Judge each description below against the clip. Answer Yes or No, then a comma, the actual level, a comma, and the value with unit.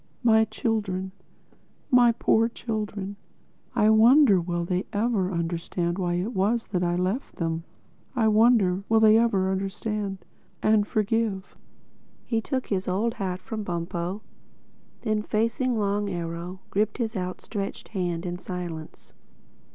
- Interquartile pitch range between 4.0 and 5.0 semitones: No, average, 3.5 semitones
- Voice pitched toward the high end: Yes, high, 200 Hz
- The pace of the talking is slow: Yes, slow, 120 wpm